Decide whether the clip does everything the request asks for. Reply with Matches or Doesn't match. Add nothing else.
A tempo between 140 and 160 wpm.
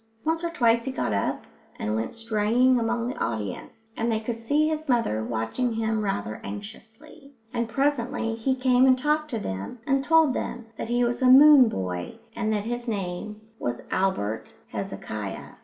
Doesn't match